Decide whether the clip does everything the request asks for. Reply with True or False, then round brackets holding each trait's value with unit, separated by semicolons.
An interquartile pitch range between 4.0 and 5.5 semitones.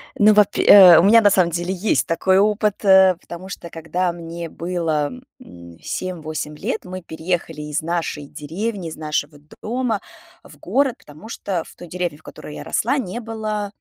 True (4.3 semitones)